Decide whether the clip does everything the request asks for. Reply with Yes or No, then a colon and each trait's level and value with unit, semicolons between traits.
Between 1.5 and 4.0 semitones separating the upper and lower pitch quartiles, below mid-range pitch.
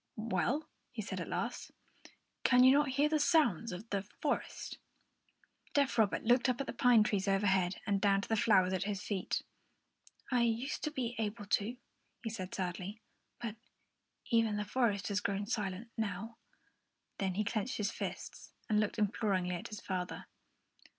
No: average, 3.3 semitones; high, 210 Hz